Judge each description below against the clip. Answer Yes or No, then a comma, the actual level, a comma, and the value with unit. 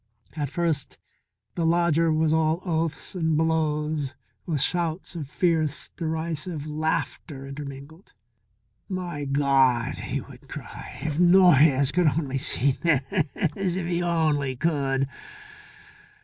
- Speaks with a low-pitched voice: No, medium, 155 Hz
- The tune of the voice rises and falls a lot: No, average, 3.0 semitones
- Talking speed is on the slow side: Yes, slow, 115 wpm